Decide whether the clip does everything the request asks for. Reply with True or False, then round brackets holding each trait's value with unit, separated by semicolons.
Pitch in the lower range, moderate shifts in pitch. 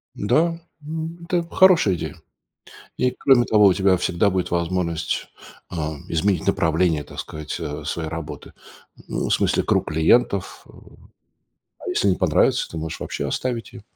False (95 Hz; 6.9 semitones)